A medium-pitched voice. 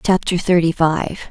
Yes: medium, 170 Hz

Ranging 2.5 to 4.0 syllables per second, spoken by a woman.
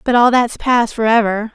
No: 4.8 syllables/s; female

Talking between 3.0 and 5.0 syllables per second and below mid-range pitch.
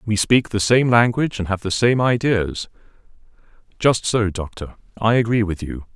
Yes: 4.9 syllables/s; low, 110 Hz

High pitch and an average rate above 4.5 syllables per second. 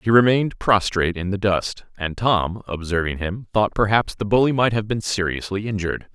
No: low, 100 Hz; 5.3 syllables/s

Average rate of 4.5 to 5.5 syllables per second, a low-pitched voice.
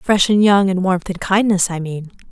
No: 4.9 syllables/s; high, 190 Hz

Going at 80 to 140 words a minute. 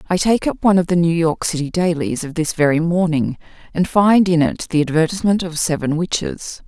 No: fast, 205 wpm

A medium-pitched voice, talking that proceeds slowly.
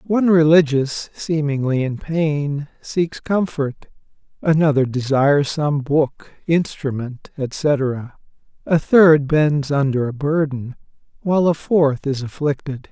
Yes: medium, 145 Hz; slow, 110 wpm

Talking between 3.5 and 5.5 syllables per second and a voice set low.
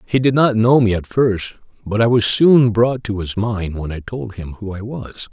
Yes: 4.5 syllables/s; low, 110 Hz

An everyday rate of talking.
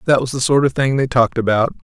No: fast, 275 wpm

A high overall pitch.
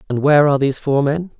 No: medium, 145 Hz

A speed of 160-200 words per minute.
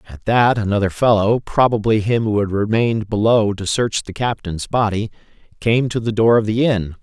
Yes: average, 190 wpm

